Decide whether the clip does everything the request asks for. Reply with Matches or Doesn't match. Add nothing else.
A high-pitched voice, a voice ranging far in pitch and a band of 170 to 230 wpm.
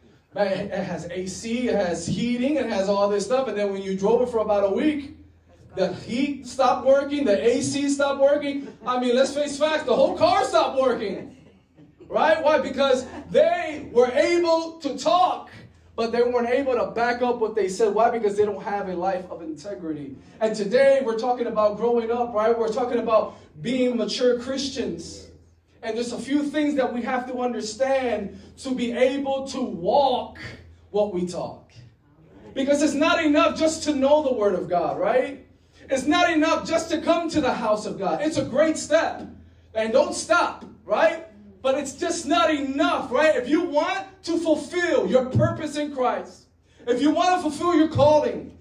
Matches